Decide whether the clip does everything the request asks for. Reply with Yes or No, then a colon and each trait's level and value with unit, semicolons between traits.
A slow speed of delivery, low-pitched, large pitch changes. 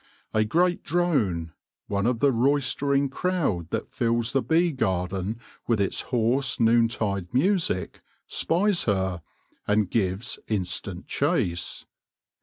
Yes: slow, 125 wpm; low, 115 Hz; wide, 6.5 semitones